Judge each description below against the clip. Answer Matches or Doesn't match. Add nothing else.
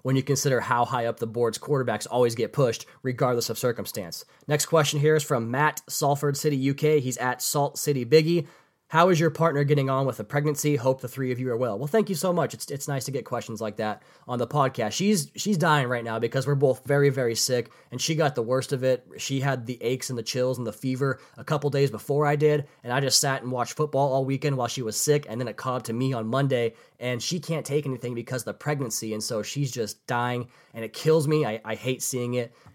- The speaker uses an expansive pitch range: Doesn't match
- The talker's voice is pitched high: Doesn't match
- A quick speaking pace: Matches